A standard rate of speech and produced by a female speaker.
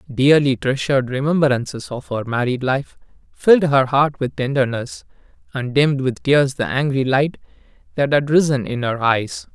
No: average, 155 wpm; male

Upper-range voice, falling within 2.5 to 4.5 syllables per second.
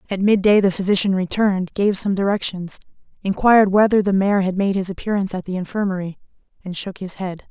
No: high, 195 Hz; 6.1 syllables/s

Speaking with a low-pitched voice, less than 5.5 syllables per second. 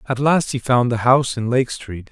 Yes: low, 125 Hz; 5.0 syllables/s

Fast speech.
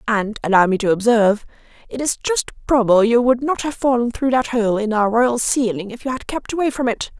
Yes: fast, 235 wpm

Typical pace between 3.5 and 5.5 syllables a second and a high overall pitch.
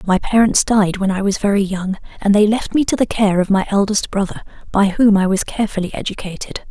No: 5.8 syllables/s; high, 200 Hz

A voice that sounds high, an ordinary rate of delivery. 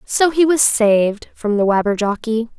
Yes: high, 230 Hz; average, 160 wpm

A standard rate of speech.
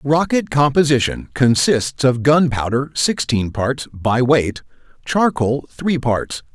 No: slow, 110 wpm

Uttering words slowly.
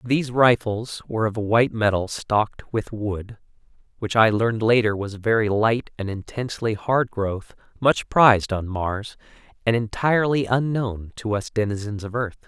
No: average, 165 wpm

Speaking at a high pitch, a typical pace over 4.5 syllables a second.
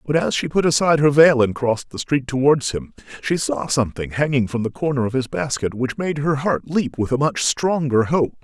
No: low, 135 Hz; 5.4 syllables/s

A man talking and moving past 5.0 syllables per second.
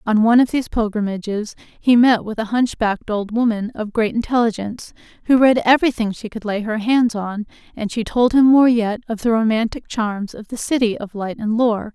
No: female; 5.4 syllables/s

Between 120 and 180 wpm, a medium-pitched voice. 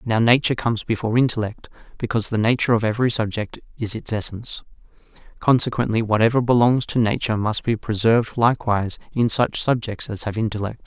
No: average, 160 wpm; low, 115 Hz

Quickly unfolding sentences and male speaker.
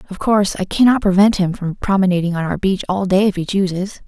No: fast, 235 wpm; female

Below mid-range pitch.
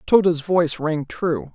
No: medium, 165 Hz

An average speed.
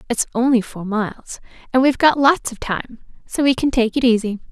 No: fast, 215 wpm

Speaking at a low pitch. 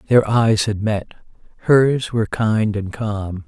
Yes: low, 110 Hz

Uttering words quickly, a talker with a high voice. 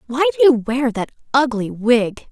No: average, 180 wpm; high, 245 Hz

